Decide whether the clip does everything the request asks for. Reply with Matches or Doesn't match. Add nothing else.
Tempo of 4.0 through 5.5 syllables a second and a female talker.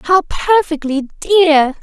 Doesn't match